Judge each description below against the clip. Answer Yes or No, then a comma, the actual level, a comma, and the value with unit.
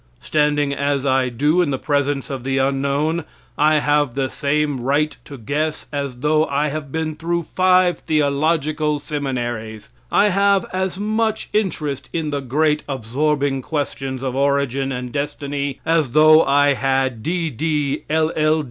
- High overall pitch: No, medium, 145 Hz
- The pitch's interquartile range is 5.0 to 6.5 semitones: No, narrow, 2.4 semitones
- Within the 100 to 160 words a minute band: Yes, average, 150 wpm